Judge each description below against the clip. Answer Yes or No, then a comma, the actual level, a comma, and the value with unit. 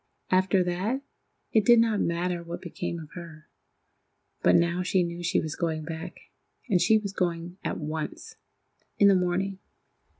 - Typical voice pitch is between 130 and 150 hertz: No, medium, 175 Hz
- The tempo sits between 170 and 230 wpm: No, average, 155 wpm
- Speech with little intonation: Yes, narrow, 2.2 semitones